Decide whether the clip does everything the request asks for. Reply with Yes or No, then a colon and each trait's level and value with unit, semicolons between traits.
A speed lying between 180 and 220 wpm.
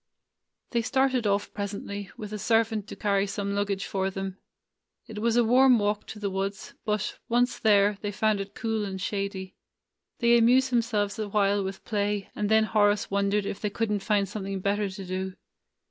Yes: average, 190 wpm